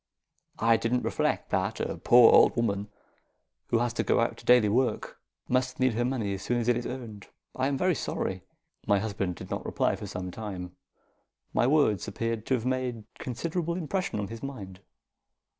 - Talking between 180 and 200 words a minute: Yes, average, 190 wpm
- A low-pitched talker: Yes, low, 120 Hz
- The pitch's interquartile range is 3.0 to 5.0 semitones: Yes, average, 3.7 semitones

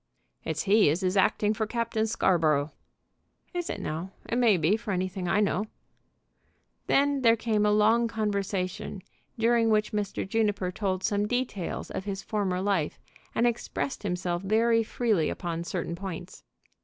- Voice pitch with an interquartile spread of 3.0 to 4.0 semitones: Yes, average, 3.5 semitones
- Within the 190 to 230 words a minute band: No, average, 155 wpm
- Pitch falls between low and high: No, high, 205 Hz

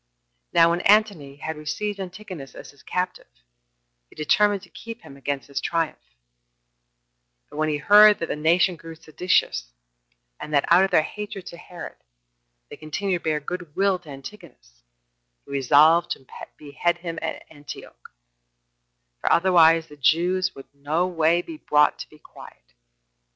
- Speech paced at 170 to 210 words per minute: No, average, 155 wpm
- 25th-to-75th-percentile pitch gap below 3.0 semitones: No, average, 3.7 semitones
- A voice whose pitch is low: No, medium, 165 Hz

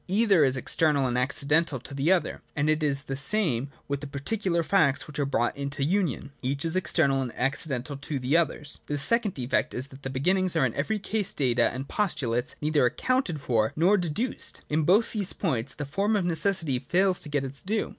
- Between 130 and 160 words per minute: No, fast, 205 wpm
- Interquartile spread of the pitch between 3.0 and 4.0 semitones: No, average, 5.2 semitones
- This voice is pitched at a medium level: Yes, medium, 150 Hz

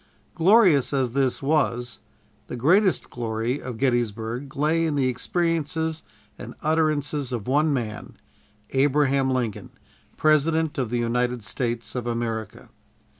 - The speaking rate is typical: No, slow, 125 wpm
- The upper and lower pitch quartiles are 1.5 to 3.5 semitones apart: No, average, 4.3 semitones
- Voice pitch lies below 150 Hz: Yes, low, 135 Hz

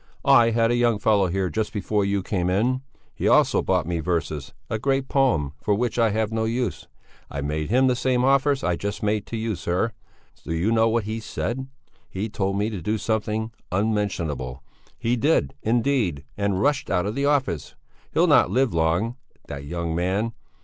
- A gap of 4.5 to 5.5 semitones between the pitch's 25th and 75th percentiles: Yes, average, 4.9 semitones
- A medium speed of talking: Yes, average, 190 wpm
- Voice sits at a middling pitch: No, low, 105 Hz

